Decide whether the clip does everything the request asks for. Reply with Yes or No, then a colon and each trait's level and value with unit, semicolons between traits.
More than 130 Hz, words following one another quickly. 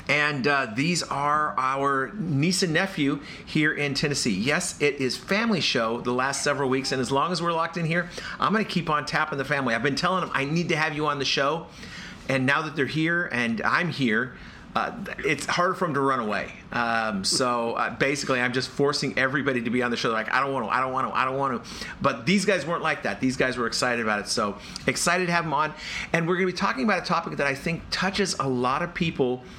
Yes: medium, 140 Hz; fast, 255 wpm